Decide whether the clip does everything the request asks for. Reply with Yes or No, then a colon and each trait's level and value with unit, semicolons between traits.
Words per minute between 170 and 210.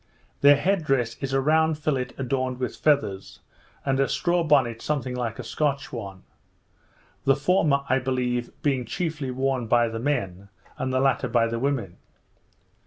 No: average, 160 wpm